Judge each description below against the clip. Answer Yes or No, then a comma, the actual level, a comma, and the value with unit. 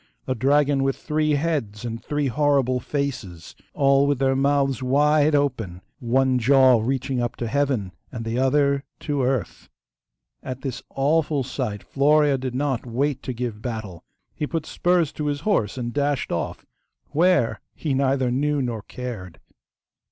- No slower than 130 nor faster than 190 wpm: Yes, average, 150 wpm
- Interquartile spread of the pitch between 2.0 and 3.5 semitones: Yes, average, 2.9 semitones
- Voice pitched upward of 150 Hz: No, low, 135 Hz